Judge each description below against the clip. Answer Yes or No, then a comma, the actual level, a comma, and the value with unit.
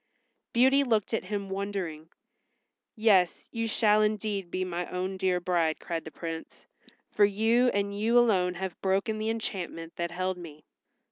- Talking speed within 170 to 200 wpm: No, average, 155 wpm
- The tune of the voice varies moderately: Yes, average, 3.3 semitones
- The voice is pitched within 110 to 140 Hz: No, high, 195 Hz